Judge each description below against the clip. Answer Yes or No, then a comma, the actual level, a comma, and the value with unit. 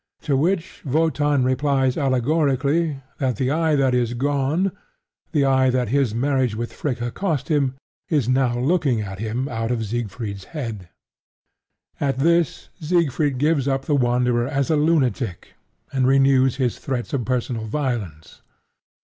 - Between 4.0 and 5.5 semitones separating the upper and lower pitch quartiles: No, average, 3.3 semitones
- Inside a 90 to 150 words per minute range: Yes, average, 145 wpm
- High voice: No, low, 135 Hz